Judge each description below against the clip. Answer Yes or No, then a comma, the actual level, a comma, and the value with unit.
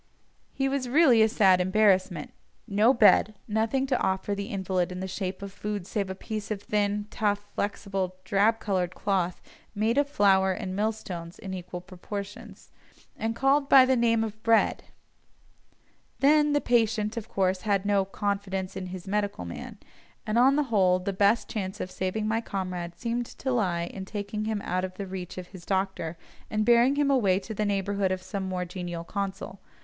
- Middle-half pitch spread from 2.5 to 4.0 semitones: Yes, average, 2.9 semitones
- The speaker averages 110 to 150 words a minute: No, average, 185 wpm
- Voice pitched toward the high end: Yes, high, 200 Hz